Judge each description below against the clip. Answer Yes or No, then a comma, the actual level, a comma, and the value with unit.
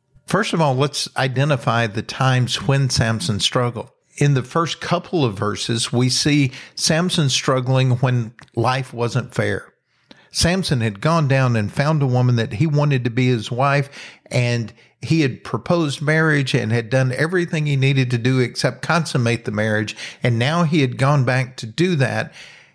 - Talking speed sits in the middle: Yes, average, 170 wpm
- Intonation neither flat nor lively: Yes, average, 3.5 semitones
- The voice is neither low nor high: No, low, 130 Hz